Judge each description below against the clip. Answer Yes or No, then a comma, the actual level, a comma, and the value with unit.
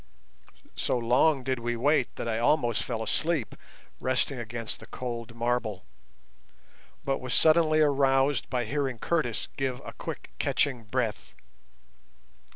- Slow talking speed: Yes, slow, 130 wpm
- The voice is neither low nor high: No, low, 125 Hz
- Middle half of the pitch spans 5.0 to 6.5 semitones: No, average, 3.0 semitones